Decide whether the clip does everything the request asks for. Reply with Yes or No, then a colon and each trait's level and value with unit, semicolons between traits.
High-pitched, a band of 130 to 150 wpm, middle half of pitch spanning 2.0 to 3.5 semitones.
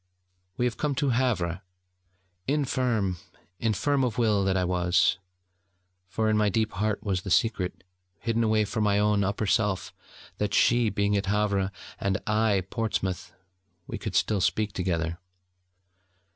No: low, 105 Hz; average, 145 wpm; average, 2.8 semitones